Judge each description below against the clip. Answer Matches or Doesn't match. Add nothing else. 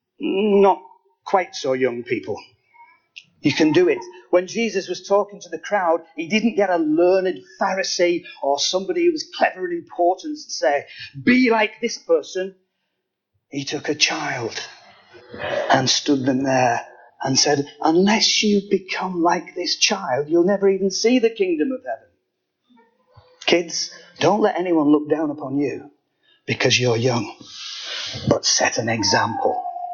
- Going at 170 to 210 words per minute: Doesn't match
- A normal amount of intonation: Doesn't match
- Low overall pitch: Doesn't match